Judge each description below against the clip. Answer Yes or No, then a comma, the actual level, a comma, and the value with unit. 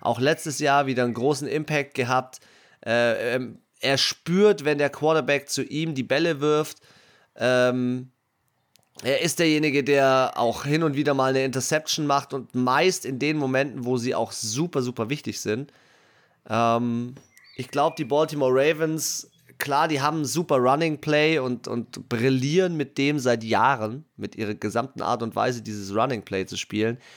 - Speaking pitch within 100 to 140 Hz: Yes, low, 135 Hz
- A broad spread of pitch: No, average, 3.5 semitones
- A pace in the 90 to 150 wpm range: No, average, 165 wpm